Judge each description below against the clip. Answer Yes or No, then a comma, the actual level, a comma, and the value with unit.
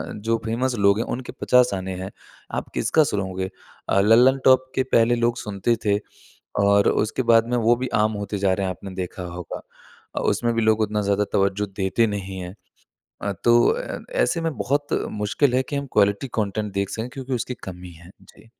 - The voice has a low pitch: Yes, low, 105 Hz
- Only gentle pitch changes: No, average, 3.6 semitones